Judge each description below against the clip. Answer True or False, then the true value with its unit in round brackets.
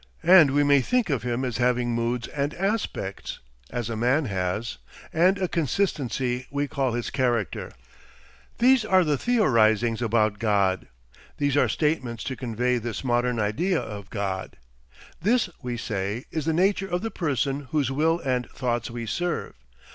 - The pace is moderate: True (155 wpm)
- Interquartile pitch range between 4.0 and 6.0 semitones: True (5.4 semitones)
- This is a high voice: False (125 Hz)